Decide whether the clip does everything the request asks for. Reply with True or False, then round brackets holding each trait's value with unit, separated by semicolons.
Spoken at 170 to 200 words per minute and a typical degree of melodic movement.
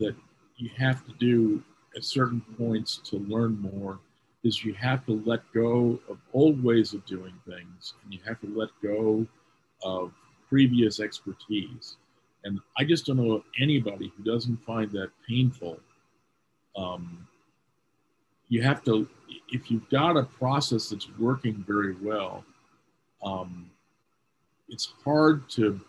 False (140 wpm; 3.6 semitones)